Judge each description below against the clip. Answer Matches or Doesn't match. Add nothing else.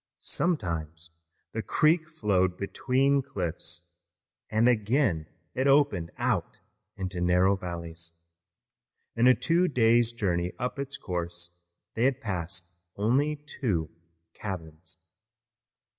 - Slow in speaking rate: Matches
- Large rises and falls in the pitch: Matches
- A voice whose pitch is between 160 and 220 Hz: Doesn't match